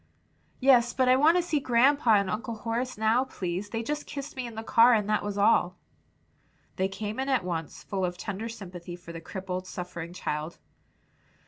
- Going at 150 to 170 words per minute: No, average, 195 wpm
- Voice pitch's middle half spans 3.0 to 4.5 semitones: No, wide, 5.5 semitones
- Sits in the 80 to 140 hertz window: No, high, 215 Hz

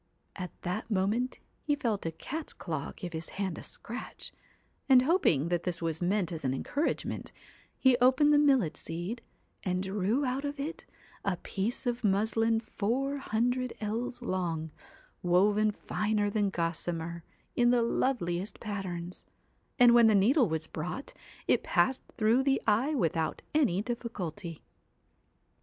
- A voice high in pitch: Yes, high, 210 Hz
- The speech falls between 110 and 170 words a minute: Yes, average, 150 wpm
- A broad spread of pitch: Yes, wide, 6.0 semitones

